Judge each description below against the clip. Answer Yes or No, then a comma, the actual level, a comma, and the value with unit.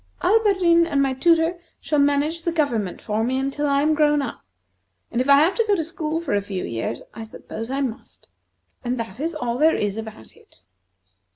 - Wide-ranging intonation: Yes, wide, 5.8 semitones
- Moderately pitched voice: No, very high, 280 Hz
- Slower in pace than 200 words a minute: No, fast, 205 wpm